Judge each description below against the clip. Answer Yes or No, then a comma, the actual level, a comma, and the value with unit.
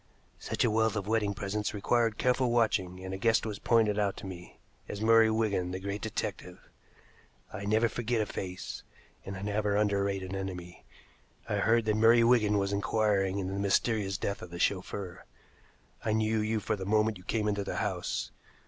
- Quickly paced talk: No, average, 185 wpm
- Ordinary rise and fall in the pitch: No, narrow, 2.2 semitones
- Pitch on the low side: Yes, low, 105 Hz